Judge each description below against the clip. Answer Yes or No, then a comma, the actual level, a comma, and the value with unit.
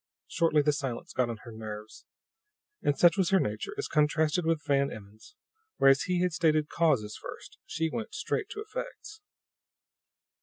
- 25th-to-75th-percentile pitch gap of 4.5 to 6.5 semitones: Yes, average, 5.2 semitones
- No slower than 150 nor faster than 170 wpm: Yes, average, 160 wpm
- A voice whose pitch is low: No, medium, 155 Hz